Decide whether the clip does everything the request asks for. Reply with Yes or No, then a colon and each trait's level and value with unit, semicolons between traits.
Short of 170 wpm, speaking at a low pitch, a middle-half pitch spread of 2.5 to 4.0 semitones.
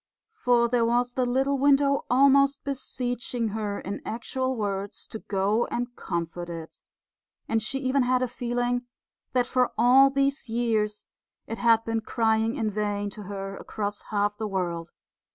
No: average, 155 wpm; high, 235 Hz; average, 3.6 semitones